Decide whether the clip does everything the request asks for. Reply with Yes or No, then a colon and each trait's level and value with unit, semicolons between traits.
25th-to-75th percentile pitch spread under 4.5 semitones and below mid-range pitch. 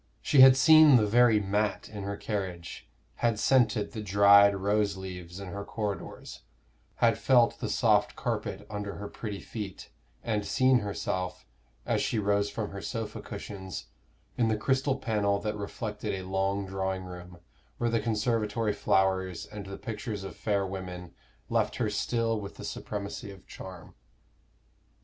Yes: average, 2.7 semitones; low, 100 Hz